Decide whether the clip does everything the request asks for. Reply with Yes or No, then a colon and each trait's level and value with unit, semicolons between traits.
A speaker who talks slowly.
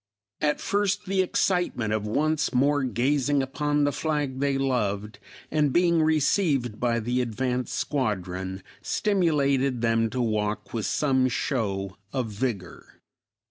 Yes: slow, 130 wpm